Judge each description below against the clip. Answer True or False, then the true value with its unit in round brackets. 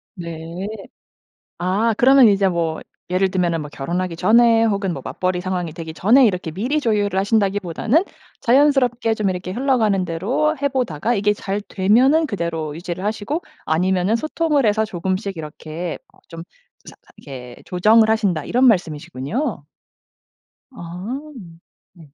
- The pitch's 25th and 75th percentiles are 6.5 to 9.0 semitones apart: False (5.1 semitones)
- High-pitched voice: True (195 Hz)